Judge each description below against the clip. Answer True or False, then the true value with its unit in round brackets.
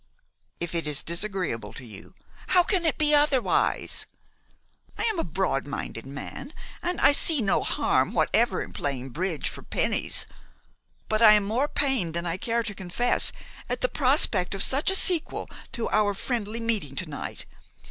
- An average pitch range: False (8.3 semitones)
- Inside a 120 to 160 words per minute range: False (175 wpm)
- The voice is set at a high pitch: True (210 Hz)